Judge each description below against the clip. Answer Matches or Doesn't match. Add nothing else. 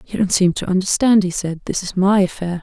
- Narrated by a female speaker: Matches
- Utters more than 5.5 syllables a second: Matches